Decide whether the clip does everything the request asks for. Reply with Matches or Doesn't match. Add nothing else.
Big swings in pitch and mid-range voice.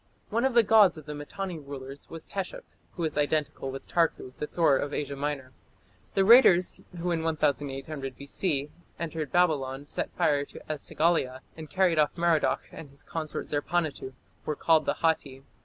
Doesn't match